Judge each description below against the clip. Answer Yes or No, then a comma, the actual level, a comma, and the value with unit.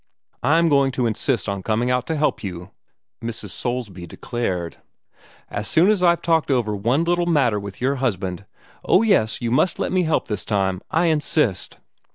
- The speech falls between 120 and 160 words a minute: No, average, 175 wpm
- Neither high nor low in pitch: No, low, 120 Hz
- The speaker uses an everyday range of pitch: No, wide, 7.8 semitones